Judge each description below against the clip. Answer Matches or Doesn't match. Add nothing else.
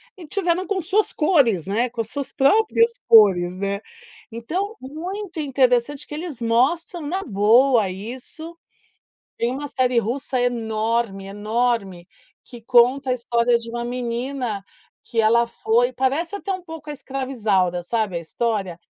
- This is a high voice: Matches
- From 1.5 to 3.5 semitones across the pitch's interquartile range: Doesn't match